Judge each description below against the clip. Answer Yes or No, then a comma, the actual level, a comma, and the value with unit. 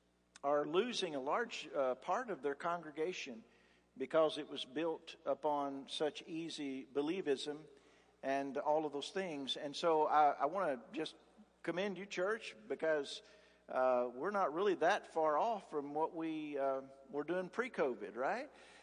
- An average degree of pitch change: Yes, average, 3.5 semitones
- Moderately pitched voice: Yes, medium, 150 Hz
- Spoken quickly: No, average, 155 wpm